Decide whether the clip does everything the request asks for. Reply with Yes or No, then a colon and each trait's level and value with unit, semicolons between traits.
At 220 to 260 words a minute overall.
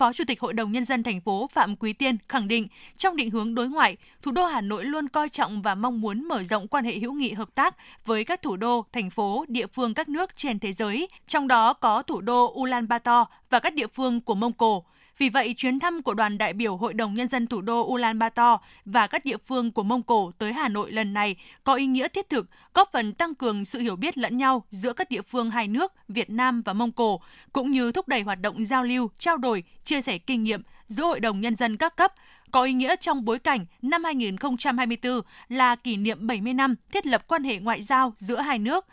Yes: average, 245 wpm